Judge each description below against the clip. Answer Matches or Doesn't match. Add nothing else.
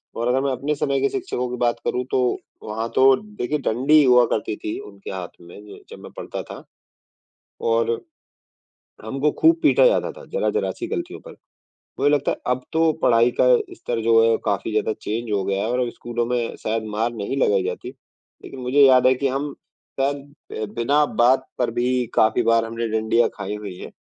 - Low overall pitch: Matches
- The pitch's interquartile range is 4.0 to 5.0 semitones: Doesn't match